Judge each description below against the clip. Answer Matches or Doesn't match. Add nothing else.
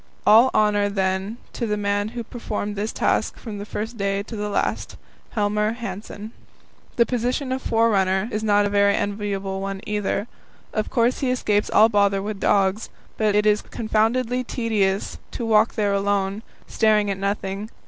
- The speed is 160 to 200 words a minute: Matches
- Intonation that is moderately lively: Doesn't match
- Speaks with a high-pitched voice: Matches